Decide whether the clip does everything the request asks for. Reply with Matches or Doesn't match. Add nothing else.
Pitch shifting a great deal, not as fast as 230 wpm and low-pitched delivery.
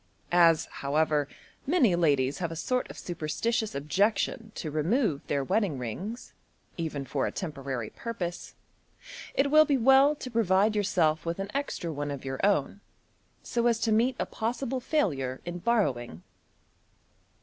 Doesn't match